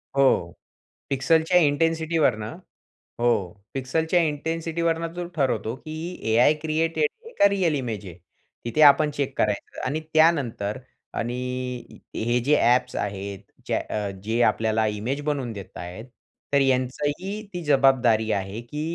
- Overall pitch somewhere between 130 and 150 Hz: Yes, medium, 140 Hz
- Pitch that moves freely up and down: Yes, wide, 5.9 semitones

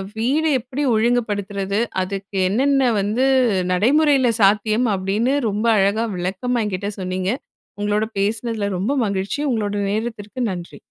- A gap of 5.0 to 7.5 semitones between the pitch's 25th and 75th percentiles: No, average, 3.5 semitones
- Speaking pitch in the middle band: No, high, 210 Hz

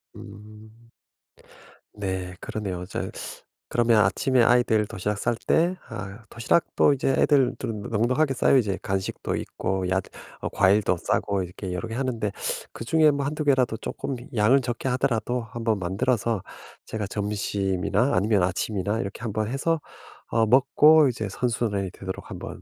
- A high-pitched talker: No, low, 110 Hz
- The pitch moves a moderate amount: Yes, average, 4.2 semitones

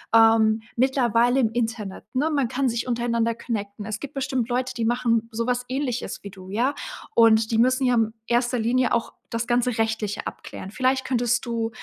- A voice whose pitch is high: Yes, high, 235 Hz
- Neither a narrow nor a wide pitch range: No, narrow, 2.0 semitones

